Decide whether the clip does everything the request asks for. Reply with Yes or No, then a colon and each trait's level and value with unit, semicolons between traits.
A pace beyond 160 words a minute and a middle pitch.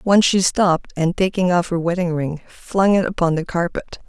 Yes: fast, 205 wpm; medium, 175 Hz